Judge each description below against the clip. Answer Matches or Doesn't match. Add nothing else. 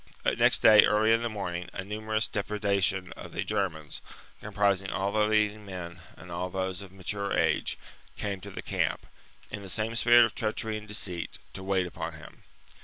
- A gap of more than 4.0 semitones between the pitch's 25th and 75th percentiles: Doesn't match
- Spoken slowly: Doesn't match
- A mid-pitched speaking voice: Doesn't match